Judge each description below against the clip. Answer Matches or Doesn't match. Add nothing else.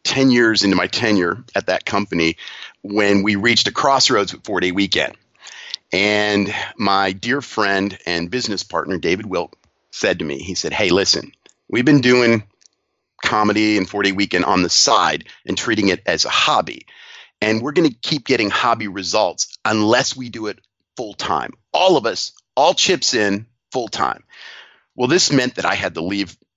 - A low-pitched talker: Matches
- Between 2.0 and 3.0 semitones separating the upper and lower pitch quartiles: Doesn't match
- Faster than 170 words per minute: Matches